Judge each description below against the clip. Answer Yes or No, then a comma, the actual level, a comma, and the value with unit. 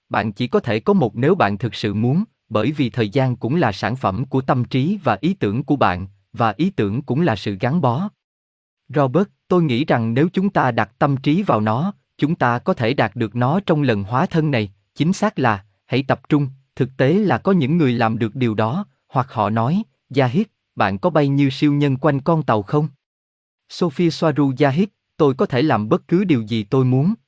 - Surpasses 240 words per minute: No, average, 220 wpm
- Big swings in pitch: Yes, wide, 6.1 semitones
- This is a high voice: No, low, 135 Hz